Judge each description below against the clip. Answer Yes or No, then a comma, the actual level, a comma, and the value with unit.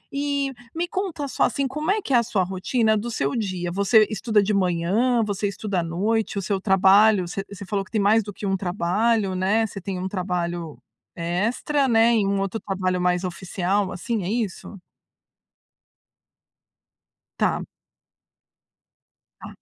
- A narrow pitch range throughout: No, average, 3.6 semitones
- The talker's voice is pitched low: No, high, 200 Hz